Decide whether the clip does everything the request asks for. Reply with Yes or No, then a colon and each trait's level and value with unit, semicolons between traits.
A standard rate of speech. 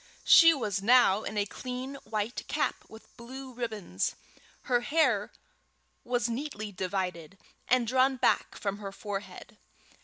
No: slow, 130 wpm